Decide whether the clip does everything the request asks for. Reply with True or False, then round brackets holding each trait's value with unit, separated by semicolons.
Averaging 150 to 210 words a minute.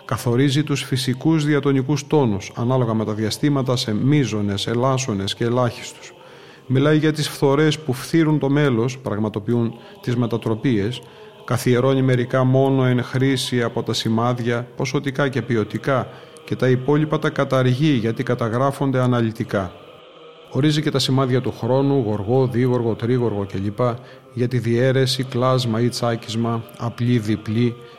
False (130 wpm)